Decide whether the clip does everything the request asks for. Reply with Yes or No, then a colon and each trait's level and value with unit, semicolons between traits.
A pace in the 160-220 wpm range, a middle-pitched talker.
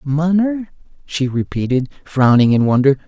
No: slow, 115 wpm; medium, 145 Hz